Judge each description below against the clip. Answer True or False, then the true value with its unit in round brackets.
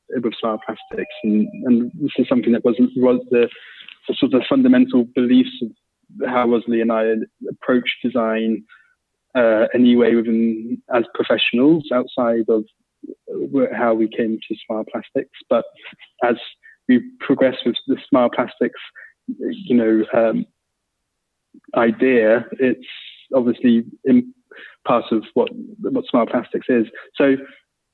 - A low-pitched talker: True (125 Hz)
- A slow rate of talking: True (130 wpm)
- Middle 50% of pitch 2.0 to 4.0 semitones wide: False (4.6 semitones)